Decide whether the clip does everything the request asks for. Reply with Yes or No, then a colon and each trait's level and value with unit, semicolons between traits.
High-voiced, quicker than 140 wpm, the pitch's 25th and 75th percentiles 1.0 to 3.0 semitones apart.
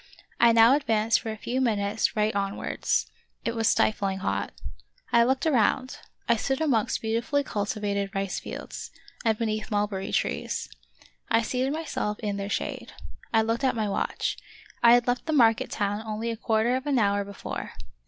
Yes: high, 225 Hz; average, 180 wpm; average, 2.7 semitones